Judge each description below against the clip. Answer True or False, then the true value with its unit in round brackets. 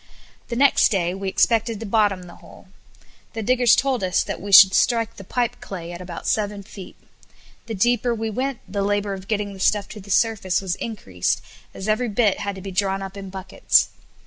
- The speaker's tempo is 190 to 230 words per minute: True (205 wpm)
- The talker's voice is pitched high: True (205 Hz)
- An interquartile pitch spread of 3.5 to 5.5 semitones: False (3.0 semitones)